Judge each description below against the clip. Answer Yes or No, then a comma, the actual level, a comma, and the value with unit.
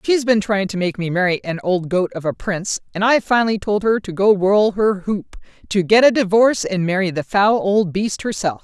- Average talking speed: No, fast, 230 wpm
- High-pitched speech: Yes, high, 200 Hz